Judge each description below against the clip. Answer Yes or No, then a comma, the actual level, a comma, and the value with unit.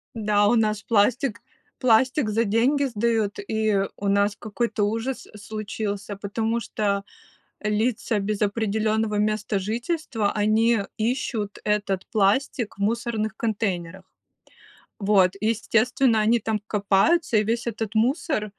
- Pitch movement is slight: Yes, narrow, 2.0 semitones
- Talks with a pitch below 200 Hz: No, high, 215 Hz